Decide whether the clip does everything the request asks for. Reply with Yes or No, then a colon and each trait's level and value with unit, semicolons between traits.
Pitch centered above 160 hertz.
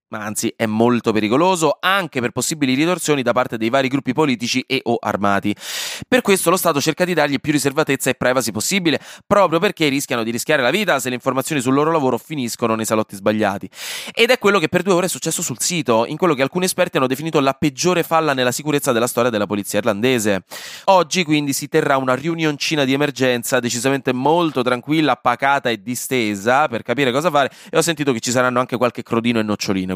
No: low, 135 Hz